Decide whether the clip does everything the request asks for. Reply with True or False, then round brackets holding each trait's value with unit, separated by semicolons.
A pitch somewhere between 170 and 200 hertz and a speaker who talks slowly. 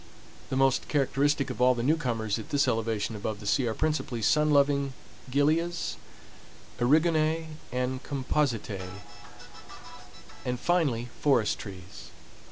False (135 Hz; 115 wpm)